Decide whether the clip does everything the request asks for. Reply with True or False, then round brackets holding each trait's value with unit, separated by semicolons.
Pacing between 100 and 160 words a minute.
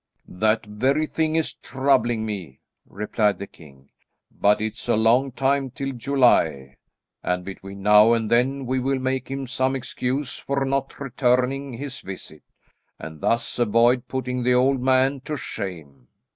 True (150 wpm)